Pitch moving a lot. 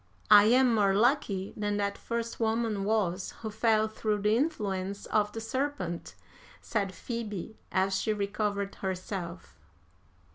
No: narrow, 2.4 semitones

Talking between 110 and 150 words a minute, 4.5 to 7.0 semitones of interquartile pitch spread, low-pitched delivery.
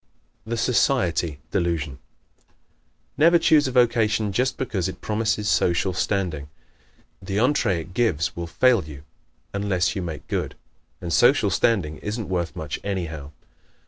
Yes: average, 140 wpm; wide, 5.4 semitones; very low, 95 Hz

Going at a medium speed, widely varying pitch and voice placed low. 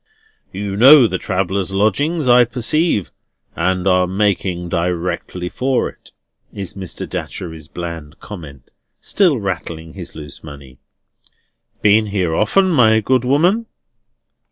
No: slow, 120 wpm; wide, 6.0 semitones; very low, 95 Hz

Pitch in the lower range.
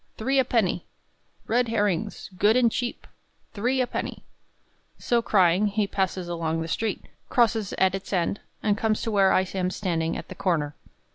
No: high, 200 Hz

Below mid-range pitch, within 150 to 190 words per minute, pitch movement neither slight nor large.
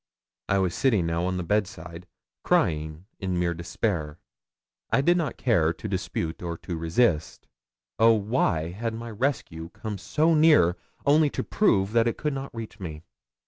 No: very low, 95 Hz; average, 160 wpm; wide, 5.8 semitones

